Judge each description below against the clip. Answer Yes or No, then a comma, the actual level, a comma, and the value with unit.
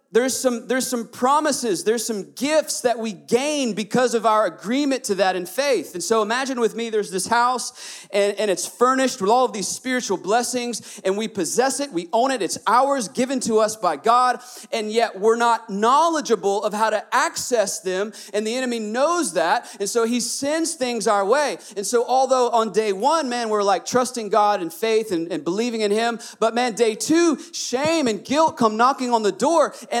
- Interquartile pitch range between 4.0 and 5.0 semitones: No, average, 3.2 semitones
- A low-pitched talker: No, high, 235 Hz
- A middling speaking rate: No, fast, 210 wpm